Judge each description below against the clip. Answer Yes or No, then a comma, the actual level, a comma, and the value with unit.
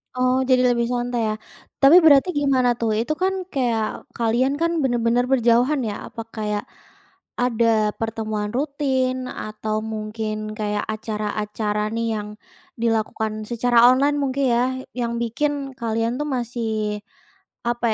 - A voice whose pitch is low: No, high, 235 Hz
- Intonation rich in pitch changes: No, average, 2.8 semitones